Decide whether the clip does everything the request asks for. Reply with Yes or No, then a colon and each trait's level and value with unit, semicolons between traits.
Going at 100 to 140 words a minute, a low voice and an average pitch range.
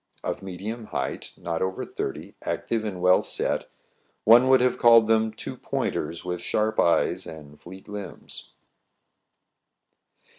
Yes: slow, 135 wpm; low, 105 Hz; average, 4.1 semitones